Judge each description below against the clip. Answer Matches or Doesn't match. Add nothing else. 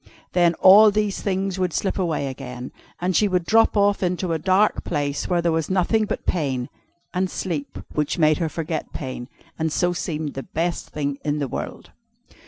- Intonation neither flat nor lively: Matches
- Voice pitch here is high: Doesn't match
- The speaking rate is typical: Matches